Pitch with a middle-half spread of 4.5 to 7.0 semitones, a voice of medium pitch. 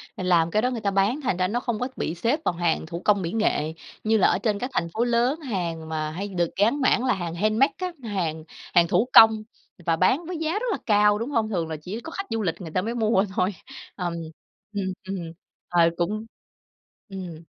No: average, 5.2 semitones; high, 205 Hz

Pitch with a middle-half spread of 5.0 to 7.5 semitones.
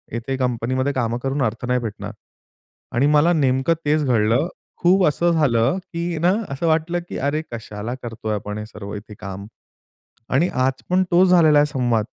Yes: wide, 5.6 semitones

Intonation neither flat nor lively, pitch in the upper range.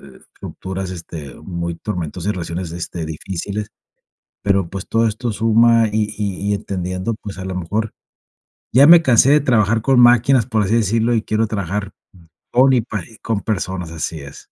No: average, 3.7 semitones; low, 105 Hz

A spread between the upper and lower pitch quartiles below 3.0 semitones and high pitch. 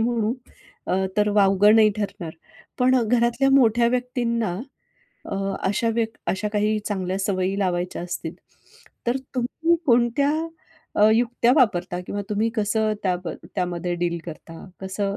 No: average, 4.0 semitones; high, 210 Hz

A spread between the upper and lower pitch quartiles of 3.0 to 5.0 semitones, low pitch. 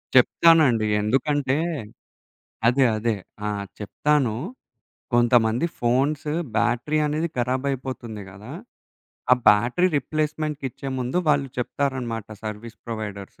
Yes: average, 4.0 semitones; low, 125 Hz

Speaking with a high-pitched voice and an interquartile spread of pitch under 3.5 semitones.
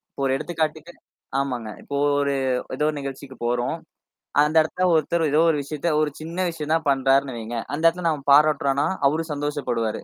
No: medium, 145 Hz; narrow, 2.6 semitones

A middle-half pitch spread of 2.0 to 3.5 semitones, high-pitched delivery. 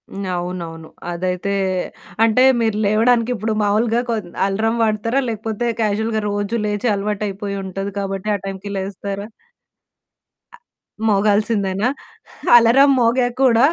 Yes: narrow, 2.6 semitones; high, 210 Hz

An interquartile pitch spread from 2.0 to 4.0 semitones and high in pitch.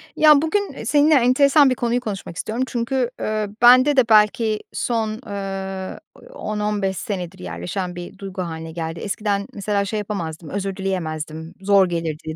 No: average, 4.7 semitones; high, 200 Hz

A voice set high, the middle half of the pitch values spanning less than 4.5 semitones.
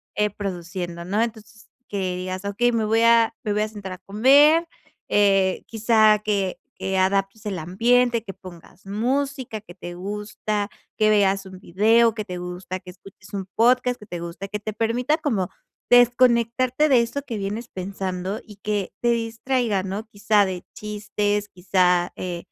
Yes: high, 210 Hz; average, 3.4 semitones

